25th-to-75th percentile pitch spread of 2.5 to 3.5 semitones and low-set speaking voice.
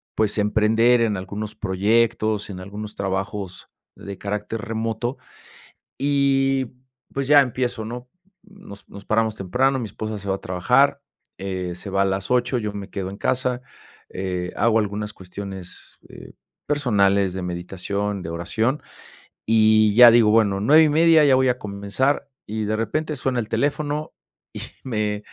No: average, 4.0 semitones; low, 110 Hz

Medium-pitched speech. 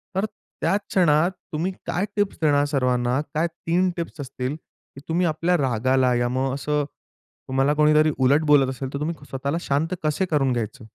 Yes: medium, 145 Hz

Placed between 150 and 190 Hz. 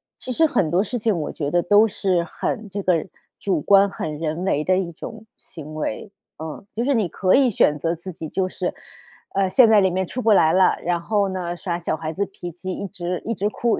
Yes: medium, 185 Hz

